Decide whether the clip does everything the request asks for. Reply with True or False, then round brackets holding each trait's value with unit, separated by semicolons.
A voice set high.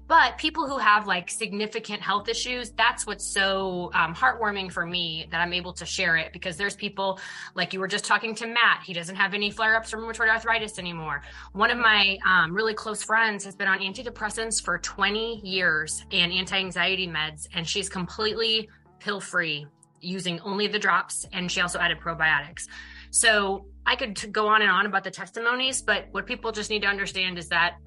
True (200 Hz)